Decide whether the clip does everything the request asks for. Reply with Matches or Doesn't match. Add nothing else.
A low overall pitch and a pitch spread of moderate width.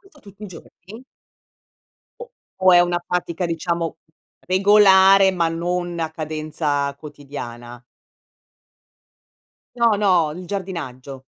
Doesn't match